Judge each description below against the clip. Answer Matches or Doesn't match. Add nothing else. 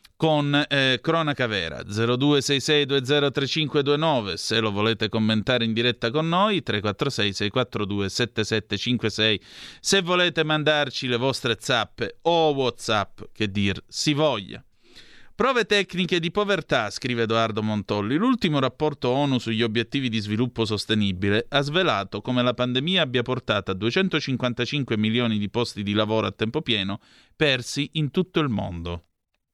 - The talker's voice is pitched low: Matches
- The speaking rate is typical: Matches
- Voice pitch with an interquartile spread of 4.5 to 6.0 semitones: Matches